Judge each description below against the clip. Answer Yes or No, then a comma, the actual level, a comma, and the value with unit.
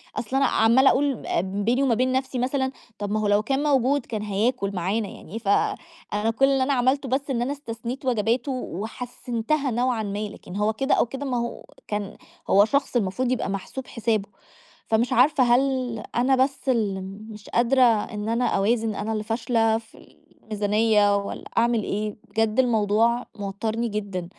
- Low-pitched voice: No, high, 230 Hz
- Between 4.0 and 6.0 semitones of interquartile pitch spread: No, average, 3.5 semitones